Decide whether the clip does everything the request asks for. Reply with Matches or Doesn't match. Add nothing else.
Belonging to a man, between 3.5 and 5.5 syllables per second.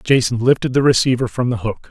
Doesn't match